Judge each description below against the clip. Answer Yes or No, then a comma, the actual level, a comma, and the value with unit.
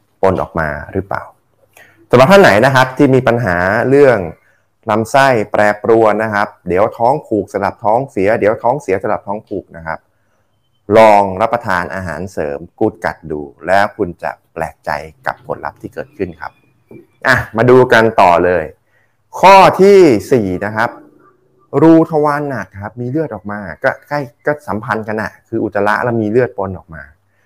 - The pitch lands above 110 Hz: No, low, 105 Hz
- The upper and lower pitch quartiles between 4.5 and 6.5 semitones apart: Yes, average, 4.9 semitones